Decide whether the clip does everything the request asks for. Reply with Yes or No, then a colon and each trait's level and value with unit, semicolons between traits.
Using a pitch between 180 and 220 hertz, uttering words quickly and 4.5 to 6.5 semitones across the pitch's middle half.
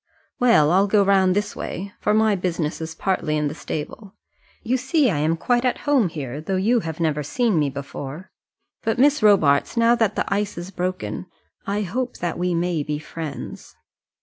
No: medium, 185 Hz; average, 190 wpm; wide, 5.6 semitones